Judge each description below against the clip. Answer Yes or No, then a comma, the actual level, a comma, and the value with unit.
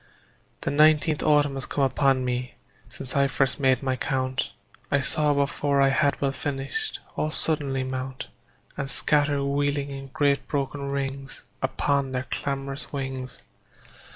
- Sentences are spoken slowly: No, average, 145 wpm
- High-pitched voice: No, medium, 140 Hz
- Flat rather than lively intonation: Yes, narrow, 1.3 semitones